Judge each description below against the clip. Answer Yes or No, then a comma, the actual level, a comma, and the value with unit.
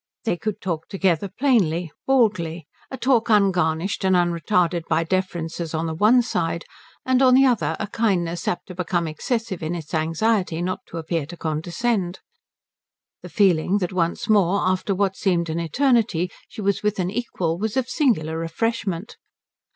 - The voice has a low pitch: No, medium, 185 Hz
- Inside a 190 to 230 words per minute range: No, average, 165 wpm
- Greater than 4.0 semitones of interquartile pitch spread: Yes, average, 4.5 semitones